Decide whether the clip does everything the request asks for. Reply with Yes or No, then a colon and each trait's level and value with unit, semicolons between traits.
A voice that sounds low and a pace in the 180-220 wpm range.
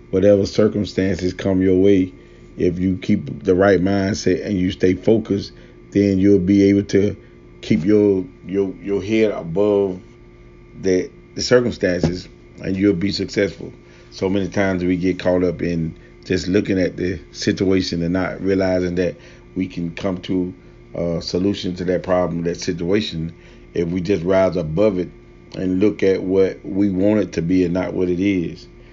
No: very low, 95 Hz; average, 170 wpm